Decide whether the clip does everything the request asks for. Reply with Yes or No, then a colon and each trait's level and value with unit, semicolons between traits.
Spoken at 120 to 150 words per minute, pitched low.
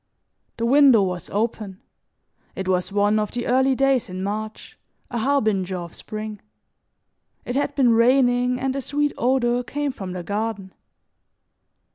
No: average, 145 wpm; high, 230 Hz